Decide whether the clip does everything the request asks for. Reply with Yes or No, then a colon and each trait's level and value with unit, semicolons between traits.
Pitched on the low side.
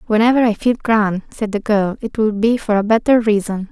No: high, 215 Hz